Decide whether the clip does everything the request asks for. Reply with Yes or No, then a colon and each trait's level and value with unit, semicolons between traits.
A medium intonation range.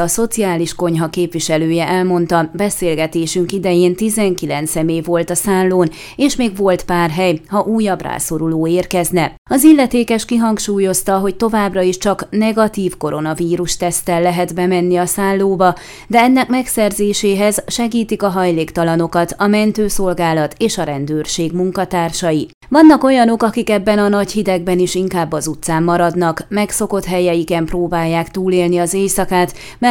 Yes: average, 3.3 semitones